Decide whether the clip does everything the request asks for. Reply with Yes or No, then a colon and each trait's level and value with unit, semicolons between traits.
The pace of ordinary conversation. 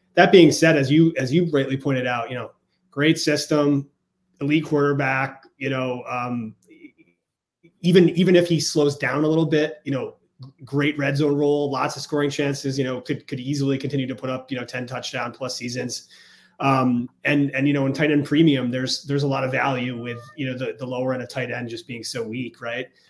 No: fast, 215 wpm